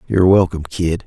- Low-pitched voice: Yes, very low, 90 Hz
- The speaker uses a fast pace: No, average, 170 wpm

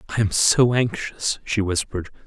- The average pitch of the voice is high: No, low, 105 Hz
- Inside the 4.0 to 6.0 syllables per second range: Yes, 5.2 syllables/s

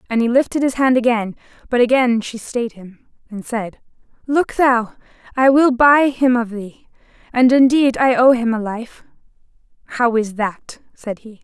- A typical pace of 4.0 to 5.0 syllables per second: Yes, 4.5 syllables/s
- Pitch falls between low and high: No, high, 240 Hz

